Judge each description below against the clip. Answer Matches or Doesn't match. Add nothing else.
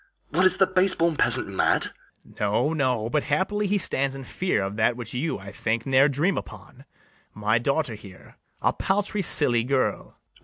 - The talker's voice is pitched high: Doesn't match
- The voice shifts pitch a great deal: Matches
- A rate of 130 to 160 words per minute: Doesn't match